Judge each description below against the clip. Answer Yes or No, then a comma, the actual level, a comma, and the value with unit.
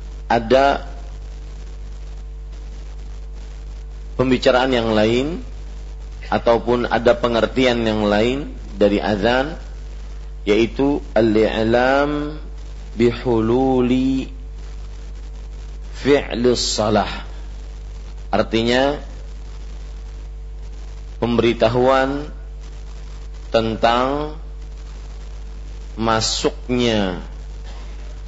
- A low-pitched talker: Yes, low, 105 Hz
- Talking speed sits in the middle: No, slow, 40 wpm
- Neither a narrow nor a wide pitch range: No, wide, 8.3 semitones